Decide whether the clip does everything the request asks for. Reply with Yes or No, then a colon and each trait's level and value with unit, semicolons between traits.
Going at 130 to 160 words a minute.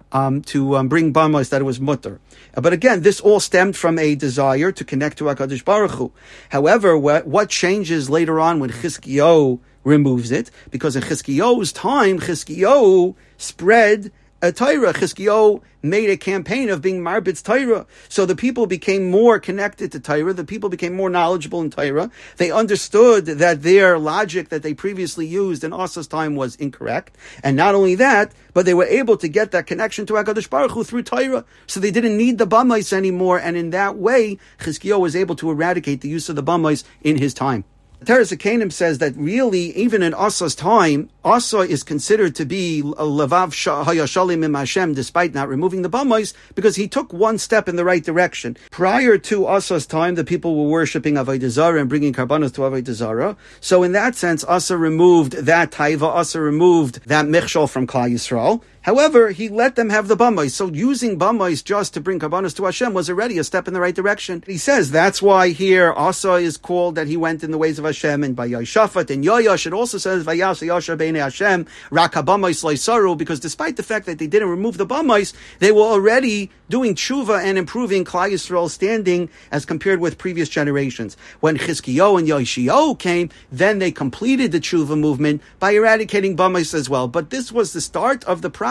No: average, 185 wpm